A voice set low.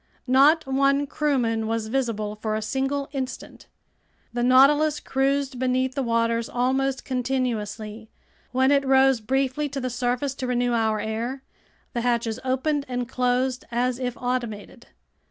No: very high, 255 Hz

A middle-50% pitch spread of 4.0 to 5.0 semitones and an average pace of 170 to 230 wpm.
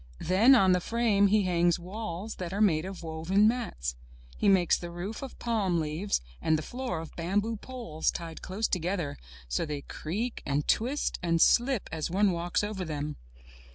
Yes: average, 4.6 semitones; average, 180 wpm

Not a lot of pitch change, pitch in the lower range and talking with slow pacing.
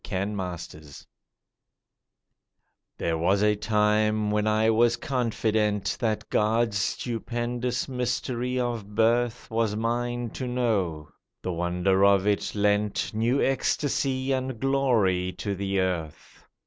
No: average, 3.5 semitones; low, 110 Hz; slow, 110 wpm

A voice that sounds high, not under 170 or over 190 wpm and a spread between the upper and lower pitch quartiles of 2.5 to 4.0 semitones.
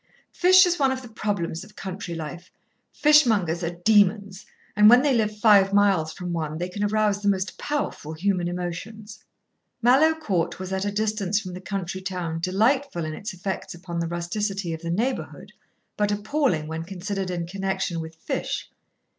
Yes: high, 195 Hz; average, 175 wpm; average, 3.7 semitones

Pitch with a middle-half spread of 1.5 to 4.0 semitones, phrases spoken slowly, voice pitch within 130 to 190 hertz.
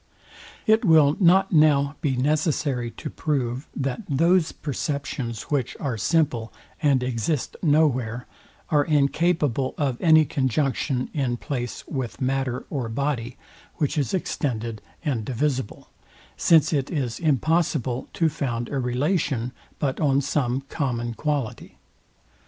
Yes: average, 3.6 semitones; slow, 125 wpm; medium, 140 Hz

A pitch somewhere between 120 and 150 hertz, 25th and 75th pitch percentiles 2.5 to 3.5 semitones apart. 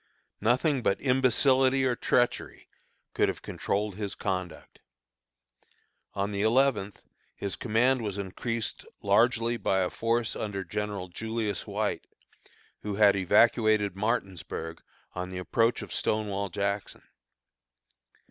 No: low, 105 Hz; average, 3.2 semitones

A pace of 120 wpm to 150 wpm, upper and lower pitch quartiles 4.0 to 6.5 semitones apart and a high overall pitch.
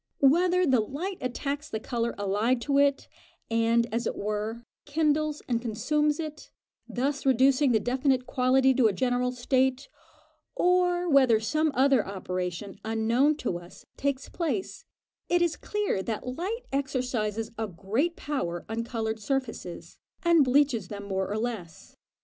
Yes: average, 145 wpm; average, 4.7 semitones; very high, 255 Hz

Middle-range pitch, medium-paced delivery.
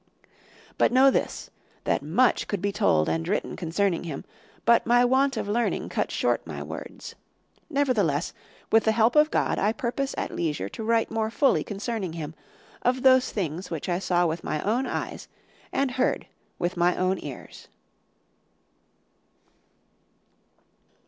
No: high, 210 Hz; average, 150 wpm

